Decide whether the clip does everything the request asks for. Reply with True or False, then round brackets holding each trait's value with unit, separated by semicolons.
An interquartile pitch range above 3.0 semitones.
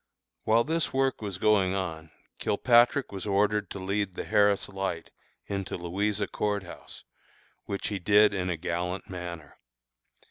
False (2.5 semitones)